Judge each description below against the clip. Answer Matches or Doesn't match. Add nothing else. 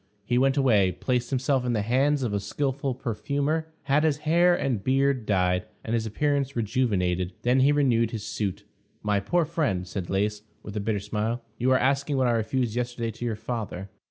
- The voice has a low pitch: Matches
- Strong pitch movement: Doesn't match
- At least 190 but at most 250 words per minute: Matches